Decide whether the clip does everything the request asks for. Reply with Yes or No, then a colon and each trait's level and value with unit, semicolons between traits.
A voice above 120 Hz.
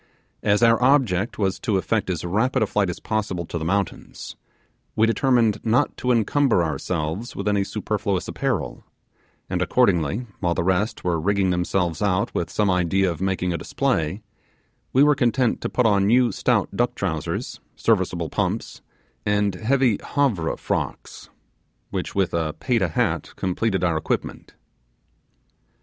No: low, 100 Hz